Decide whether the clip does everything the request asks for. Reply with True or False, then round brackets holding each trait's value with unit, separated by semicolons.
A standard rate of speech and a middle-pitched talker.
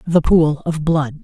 True (195 wpm; 155 Hz)